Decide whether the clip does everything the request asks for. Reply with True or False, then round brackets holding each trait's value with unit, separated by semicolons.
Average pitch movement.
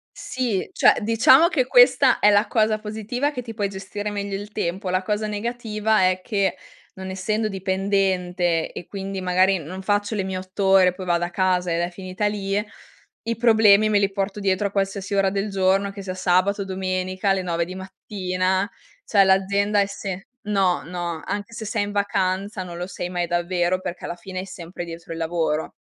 False (2.0 semitones)